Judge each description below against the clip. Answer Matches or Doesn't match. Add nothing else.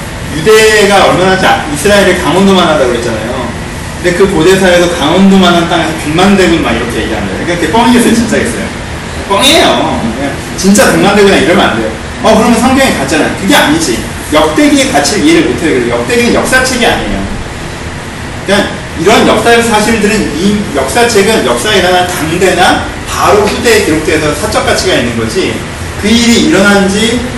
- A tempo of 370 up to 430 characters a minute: Matches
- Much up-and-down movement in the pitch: Doesn't match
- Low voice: Doesn't match